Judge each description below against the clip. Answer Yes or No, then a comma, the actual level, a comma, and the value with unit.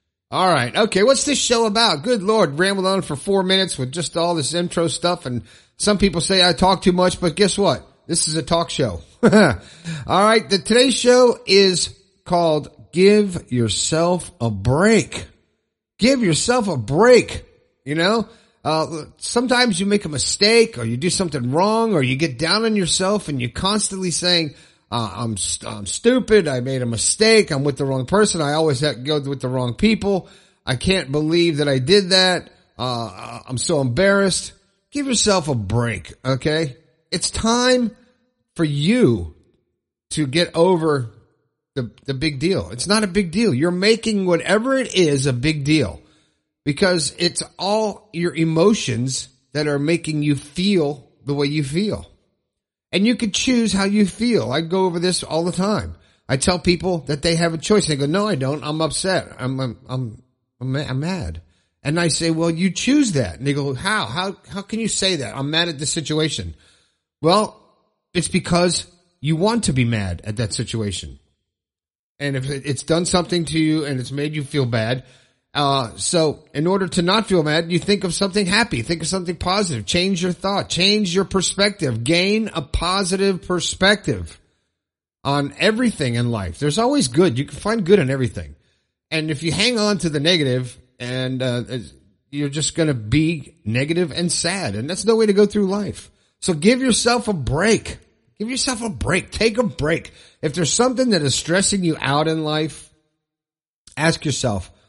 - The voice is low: No, medium, 165 Hz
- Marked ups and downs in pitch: Yes, wide, 6.6 semitones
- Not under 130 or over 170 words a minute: No, average, 185 wpm